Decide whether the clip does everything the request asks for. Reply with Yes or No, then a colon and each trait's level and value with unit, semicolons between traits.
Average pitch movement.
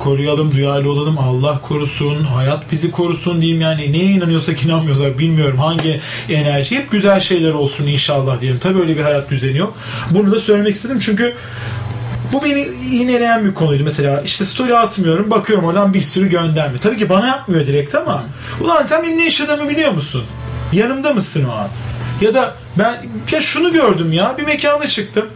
No: wide, 7.0 semitones